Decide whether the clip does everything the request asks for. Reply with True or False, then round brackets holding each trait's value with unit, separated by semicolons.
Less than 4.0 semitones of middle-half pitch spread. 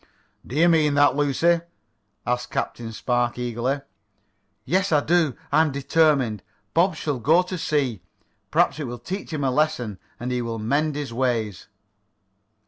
False (4.4 semitones)